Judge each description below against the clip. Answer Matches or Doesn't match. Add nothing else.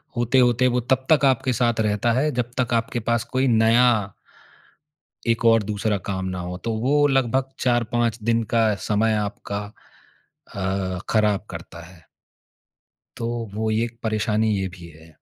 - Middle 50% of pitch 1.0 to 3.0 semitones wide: Matches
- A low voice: Matches